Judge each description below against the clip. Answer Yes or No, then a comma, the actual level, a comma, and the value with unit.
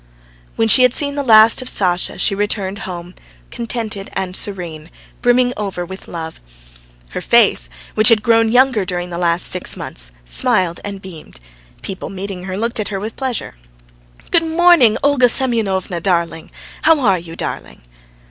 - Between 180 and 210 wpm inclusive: No, average, 160 wpm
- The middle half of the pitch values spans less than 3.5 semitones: No, average, 4.9 semitones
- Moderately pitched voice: No, high, 200 Hz